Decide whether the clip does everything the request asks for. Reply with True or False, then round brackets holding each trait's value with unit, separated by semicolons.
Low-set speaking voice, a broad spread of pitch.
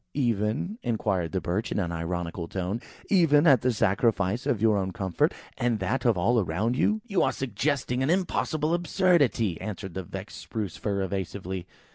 True (105 Hz; 5.9 semitones)